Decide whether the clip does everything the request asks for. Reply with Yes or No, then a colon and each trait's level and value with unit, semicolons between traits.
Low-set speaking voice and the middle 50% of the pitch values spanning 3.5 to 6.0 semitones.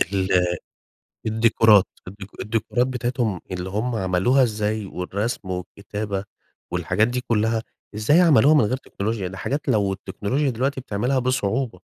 Yes: low, 110 Hz; average, 4.2 semitones